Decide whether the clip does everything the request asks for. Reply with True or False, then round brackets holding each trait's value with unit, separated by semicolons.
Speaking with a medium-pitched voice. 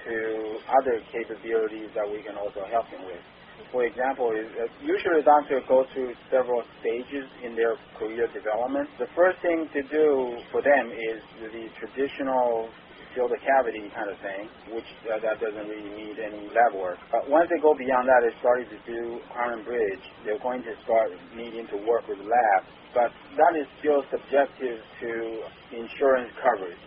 False (120 Hz)